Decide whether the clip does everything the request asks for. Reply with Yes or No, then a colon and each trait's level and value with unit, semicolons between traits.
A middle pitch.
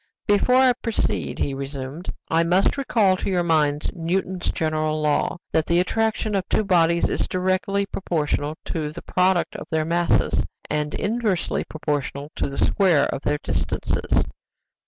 Yes: medium, 170 Hz